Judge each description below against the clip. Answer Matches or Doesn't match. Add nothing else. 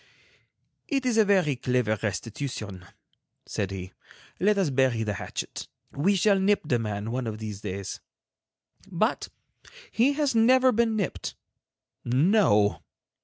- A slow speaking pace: Matches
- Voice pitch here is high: Doesn't match